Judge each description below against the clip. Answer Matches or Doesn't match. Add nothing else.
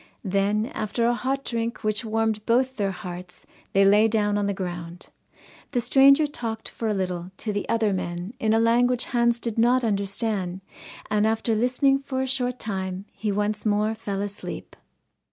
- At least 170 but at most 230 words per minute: Matches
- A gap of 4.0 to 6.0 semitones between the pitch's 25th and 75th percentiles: Doesn't match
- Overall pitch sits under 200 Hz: Doesn't match